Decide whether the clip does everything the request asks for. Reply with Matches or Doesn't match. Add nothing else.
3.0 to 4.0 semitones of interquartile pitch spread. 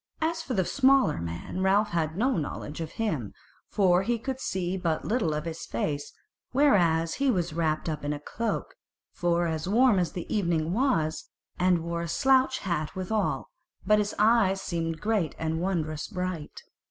Doesn't match